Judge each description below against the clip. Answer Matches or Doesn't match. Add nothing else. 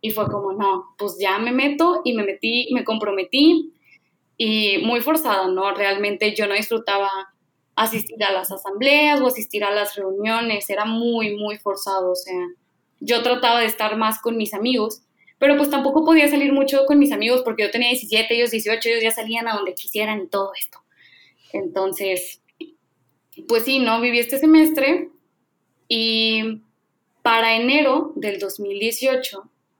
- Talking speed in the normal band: Matches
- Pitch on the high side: Matches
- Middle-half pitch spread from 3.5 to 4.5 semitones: Matches